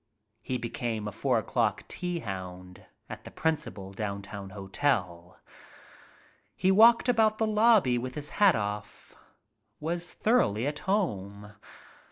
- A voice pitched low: Yes, low, 120 Hz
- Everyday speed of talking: No, slow, 125 wpm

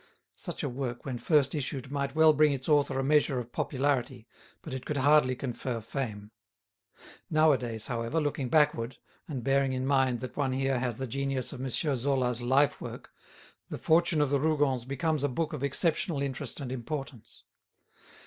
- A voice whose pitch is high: No, low, 135 Hz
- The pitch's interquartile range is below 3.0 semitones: Yes, narrow, 2.6 semitones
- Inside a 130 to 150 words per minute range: No, average, 170 wpm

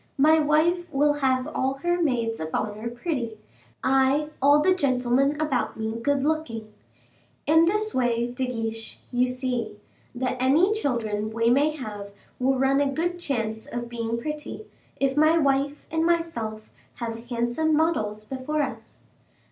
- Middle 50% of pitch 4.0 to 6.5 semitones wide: Yes, average, 4.5 semitones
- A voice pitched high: Yes, very high, 265 Hz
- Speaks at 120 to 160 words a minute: Yes, average, 150 wpm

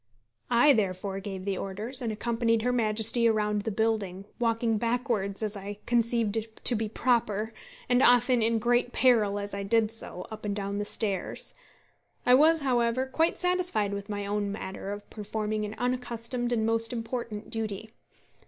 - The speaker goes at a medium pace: Yes, average, 165 wpm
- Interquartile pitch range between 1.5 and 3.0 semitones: Yes, average, 2.7 semitones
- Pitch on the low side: No, high, 225 Hz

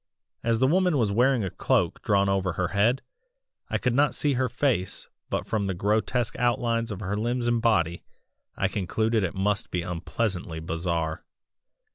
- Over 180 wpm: No, average, 170 wpm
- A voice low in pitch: Yes, low, 105 Hz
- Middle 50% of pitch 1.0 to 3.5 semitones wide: No, average, 4.5 semitones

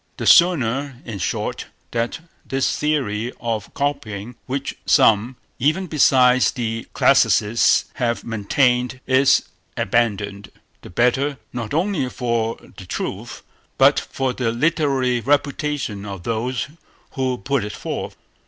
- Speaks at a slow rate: Yes, slow, 120 wpm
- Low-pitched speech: Yes, low, 125 Hz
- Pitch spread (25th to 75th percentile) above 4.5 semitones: No, average, 3.5 semitones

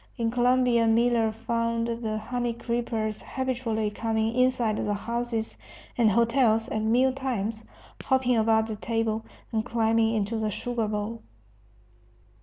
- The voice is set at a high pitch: Yes, high, 230 Hz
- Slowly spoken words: Yes, slow, 130 wpm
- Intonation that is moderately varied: No, narrow, 1.5 semitones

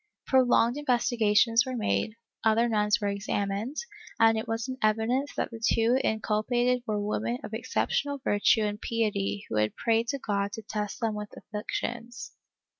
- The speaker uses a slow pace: No, average, 160 wpm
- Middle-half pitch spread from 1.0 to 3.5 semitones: Yes, narrow, 2.5 semitones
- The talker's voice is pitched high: Yes, high, 225 Hz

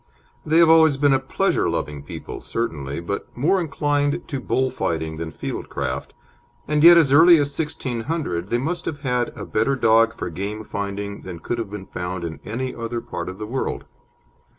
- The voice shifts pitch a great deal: Yes, wide, 6.9 semitones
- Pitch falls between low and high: No, low, 120 Hz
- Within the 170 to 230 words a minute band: Yes, average, 190 wpm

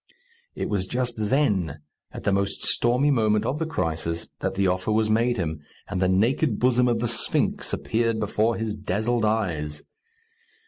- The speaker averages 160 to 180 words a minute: Yes, average, 170 wpm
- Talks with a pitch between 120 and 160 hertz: No, low, 110 Hz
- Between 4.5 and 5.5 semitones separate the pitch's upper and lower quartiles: No, average, 4.1 semitones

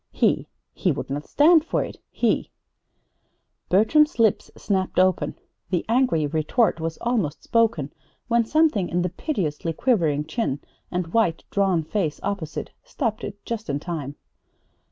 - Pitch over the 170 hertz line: Yes, high, 190 Hz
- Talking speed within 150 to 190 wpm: No, average, 140 wpm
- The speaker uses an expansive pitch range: Yes, wide, 6.3 semitones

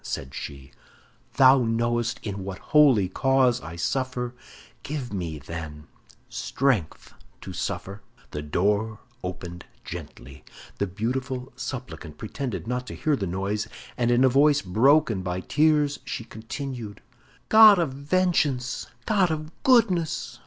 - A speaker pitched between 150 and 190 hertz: No, low, 120 Hz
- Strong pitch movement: Yes, wide, 6.5 semitones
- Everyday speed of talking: No, slow, 130 wpm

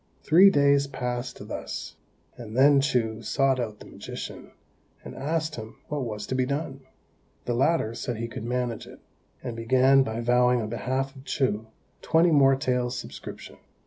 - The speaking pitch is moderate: No, low, 130 Hz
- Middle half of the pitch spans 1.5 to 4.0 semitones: Yes, average, 2.9 semitones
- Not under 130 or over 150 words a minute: No, average, 165 wpm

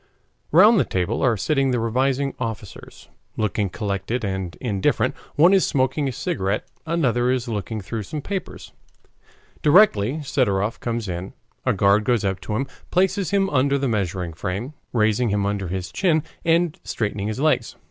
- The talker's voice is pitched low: Yes, low, 115 Hz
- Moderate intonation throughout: No, wide, 5.8 semitones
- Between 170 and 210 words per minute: No, average, 160 wpm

